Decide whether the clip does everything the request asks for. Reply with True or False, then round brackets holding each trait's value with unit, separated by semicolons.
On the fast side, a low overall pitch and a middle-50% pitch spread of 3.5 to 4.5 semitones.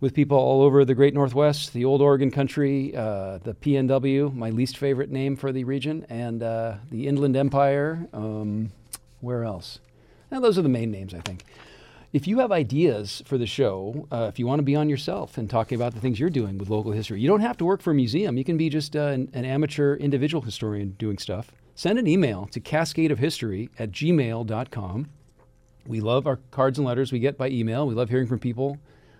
True (215 wpm; 130 Hz; 3.9 semitones)